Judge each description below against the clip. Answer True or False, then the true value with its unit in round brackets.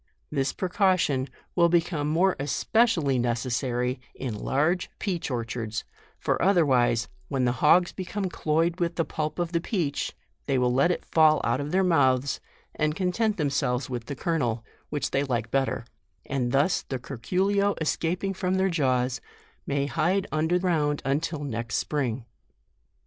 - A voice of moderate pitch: True (150 Hz)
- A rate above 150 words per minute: True (160 wpm)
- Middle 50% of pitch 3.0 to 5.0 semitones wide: False (5.4 semitones)